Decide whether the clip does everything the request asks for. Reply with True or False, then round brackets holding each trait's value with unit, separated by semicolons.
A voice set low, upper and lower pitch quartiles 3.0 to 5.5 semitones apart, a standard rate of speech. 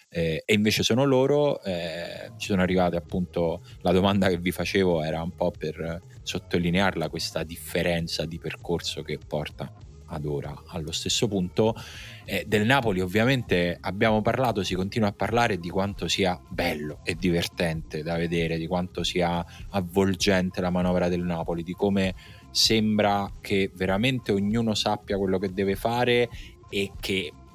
True (95 Hz; 3.5 semitones; 150 wpm)